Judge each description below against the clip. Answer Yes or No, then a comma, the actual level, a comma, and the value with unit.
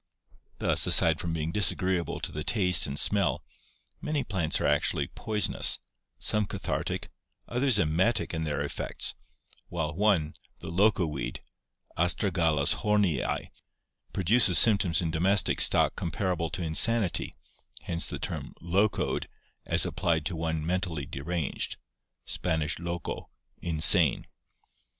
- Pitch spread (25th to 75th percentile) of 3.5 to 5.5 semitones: Yes, average, 3.8 semitones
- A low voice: Yes, very low, 85 Hz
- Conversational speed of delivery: No, slow, 120 wpm